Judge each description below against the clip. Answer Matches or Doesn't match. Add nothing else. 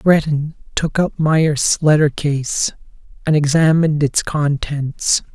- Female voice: Doesn't match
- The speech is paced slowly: Matches